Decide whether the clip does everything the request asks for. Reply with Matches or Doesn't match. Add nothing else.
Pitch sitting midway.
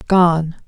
Matches